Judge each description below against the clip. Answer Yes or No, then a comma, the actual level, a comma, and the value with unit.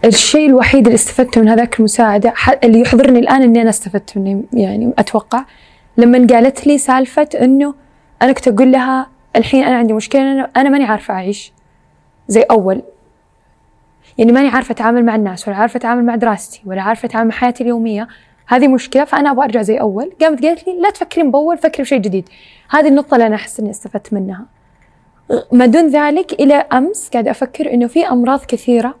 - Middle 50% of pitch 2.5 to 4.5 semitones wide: Yes, average, 3.6 semitones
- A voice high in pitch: Yes, high, 245 Hz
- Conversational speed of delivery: No, fast, 180 wpm